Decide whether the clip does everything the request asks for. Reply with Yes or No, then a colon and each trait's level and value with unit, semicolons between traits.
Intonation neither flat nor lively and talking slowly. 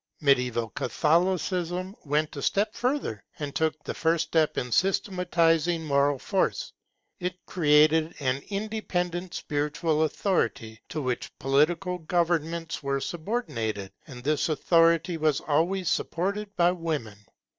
Yes: average, 3.7 semitones; slow, 120 wpm